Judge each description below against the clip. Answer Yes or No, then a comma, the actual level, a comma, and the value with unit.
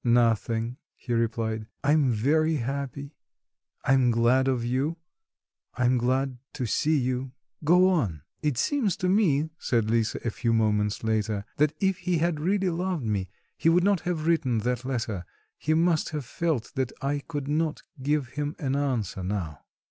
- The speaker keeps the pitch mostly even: No, average, 5.3 semitones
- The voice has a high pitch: No, low, 135 Hz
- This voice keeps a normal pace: Yes, average, 165 wpm